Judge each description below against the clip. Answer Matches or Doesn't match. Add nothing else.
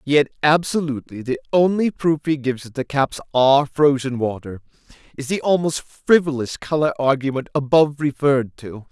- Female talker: Doesn't match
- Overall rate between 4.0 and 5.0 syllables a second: Doesn't match